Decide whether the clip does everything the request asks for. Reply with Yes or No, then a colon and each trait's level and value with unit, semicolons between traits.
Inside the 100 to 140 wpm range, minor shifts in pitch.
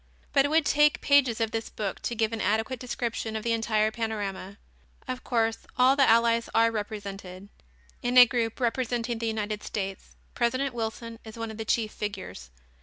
No: average, 180 wpm; narrow, 2.0 semitones